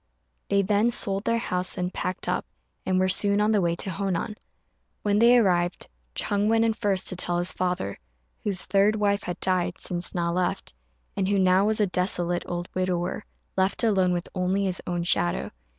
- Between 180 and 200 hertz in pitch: Yes, medium, 185 Hz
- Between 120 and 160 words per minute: No, average, 190 wpm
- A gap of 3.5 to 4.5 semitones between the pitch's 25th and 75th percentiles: No, narrow, 2.4 semitones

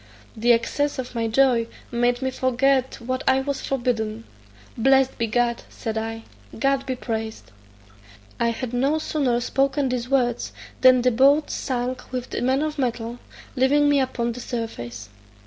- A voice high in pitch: Yes, very high, 250 Hz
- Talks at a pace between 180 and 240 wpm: No, average, 160 wpm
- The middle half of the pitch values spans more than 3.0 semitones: No, narrow, 2.4 semitones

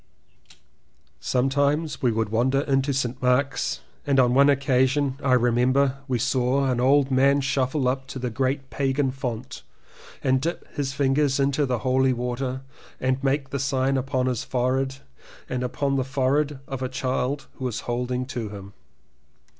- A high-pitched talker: No, low, 130 Hz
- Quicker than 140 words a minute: Yes, average, 160 wpm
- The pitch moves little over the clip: Yes, narrow, 1.5 semitones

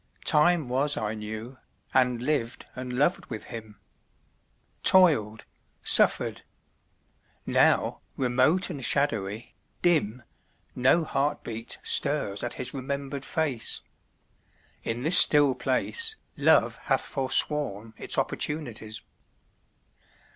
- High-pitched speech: No, low, 130 Hz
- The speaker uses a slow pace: Yes, slow, 95 wpm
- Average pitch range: Yes, average, 4.6 semitones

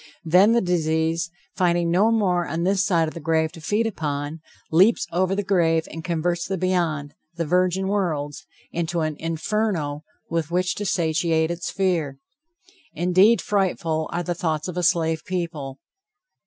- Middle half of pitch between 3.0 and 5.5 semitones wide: No, narrow, 2.5 semitones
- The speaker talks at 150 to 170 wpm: Yes, average, 160 wpm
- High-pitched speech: No, medium, 170 Hz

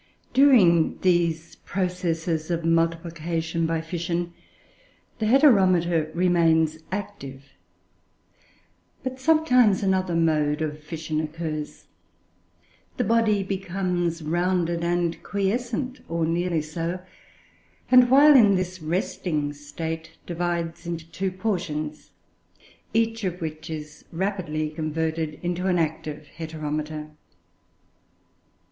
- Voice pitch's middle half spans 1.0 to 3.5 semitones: Yes, average, 2.9 semitones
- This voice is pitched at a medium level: Yes, medium, 170 Hz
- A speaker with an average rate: No, slow, 100 wpm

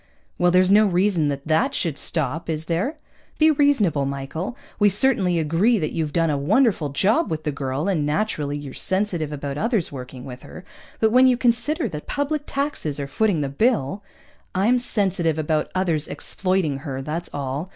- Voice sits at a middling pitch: Yes, medium, 170 Hz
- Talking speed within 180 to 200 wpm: Yes, average, 185 wpm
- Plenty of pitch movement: Yes, wide, 6.4 semitones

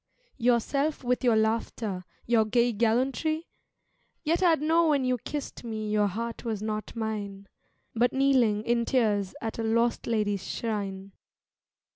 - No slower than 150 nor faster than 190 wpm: No, average, 140 wpm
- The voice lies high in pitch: Yes, high, 230 Hz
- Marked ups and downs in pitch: No, average, 3.0 semitones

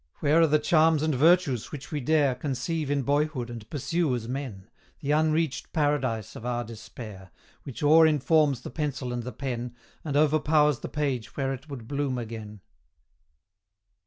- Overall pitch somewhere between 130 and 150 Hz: Yes, medium, 140 Hz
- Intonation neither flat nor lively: Yes, average, 3.8 semitones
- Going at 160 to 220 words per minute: Yes, average, 165 wpm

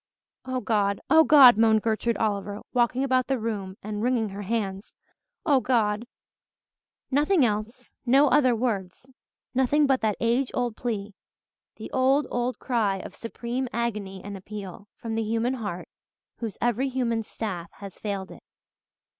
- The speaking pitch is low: No, high, 230 Hz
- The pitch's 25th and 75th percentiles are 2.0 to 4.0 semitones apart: Yes, average, 3.6 semitones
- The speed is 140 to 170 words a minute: Yes, average, 150 wpm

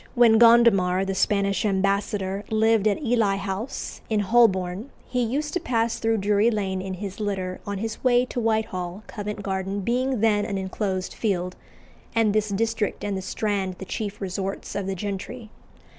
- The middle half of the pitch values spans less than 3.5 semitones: Yes, average, 2.7 semitones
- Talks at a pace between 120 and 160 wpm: No, average, 170 wpm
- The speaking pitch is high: Yes, high, 205 Hz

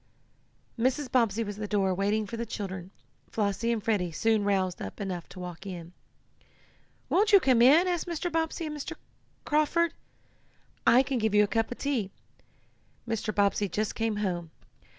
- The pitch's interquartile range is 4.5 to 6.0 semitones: Yes, average, 5.1 semitones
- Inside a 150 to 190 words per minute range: Yes, average, 170 wpm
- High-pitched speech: Yes, high, 220 Hz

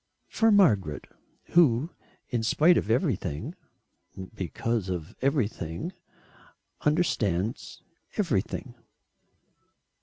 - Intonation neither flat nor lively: No, wide, 9.0 semitones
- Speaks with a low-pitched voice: Yes, low, 115 Hz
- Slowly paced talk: Yes, slow, 70 wpm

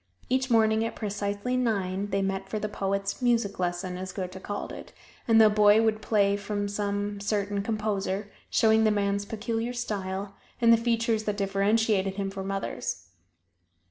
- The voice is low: No, high, 205 Hz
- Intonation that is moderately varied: No, narrow, 2.0 semitones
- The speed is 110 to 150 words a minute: No, average, 165 wpm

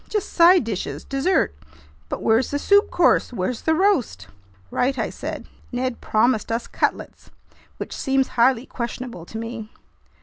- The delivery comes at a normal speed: Yes, average, 145 wpm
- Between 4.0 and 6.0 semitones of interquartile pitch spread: Yes, average, 4.3 semitones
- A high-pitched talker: Yes, very high, 250 Hz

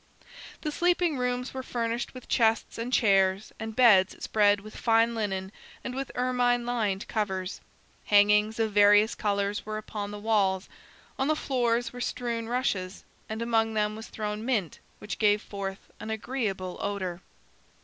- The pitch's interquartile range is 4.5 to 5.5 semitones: No, average, 3.0 semitones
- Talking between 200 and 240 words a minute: No, average, 155 wpm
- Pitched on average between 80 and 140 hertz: No, high, 220 Hz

